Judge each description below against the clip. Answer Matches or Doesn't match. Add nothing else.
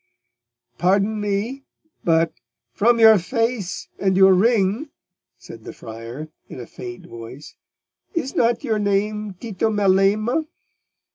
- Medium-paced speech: Doesn't match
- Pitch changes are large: Doesn't match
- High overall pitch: Matches